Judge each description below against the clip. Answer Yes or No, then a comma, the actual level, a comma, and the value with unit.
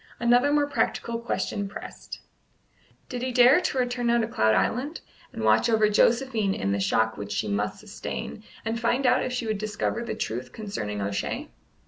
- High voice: Yes, high, 225 Hz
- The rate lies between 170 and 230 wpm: Yes, average, 180 wpm